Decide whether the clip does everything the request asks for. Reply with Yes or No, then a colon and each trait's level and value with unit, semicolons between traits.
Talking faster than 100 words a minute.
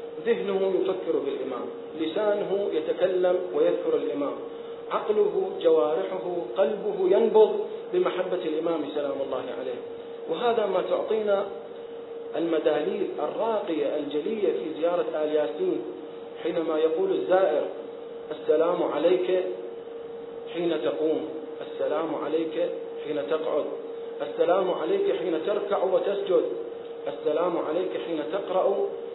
No: average, 95 wpm